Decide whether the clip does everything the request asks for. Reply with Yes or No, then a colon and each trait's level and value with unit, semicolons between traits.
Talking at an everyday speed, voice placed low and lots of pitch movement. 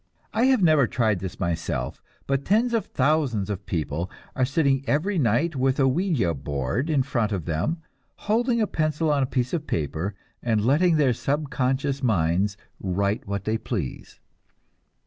Yes: average, 160 wpm; low, 130 Hz; wide, 7.5 semitones